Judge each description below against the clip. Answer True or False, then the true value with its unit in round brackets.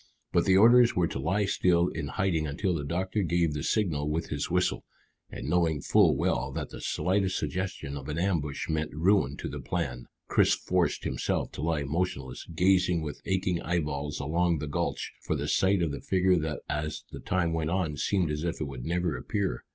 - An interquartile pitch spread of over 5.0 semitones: False (3.8 semitones)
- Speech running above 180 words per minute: True (200 wpm)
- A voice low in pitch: True (85 Hz)